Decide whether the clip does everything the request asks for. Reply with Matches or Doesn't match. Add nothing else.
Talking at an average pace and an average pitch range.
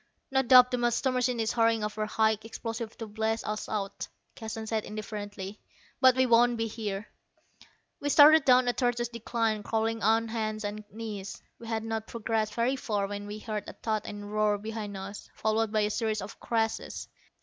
Doesn't match